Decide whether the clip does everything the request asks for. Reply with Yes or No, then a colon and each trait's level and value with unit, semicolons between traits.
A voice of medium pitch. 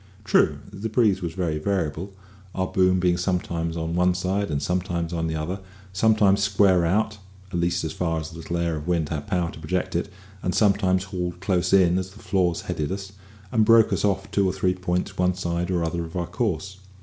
No: very low, 90 Hz